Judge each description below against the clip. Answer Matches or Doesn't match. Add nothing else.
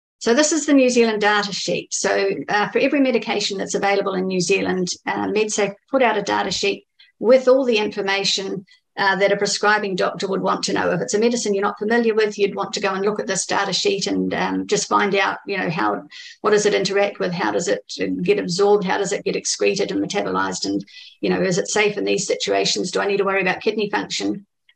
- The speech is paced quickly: Matches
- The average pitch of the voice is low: Doesn't match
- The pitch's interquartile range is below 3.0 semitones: Matches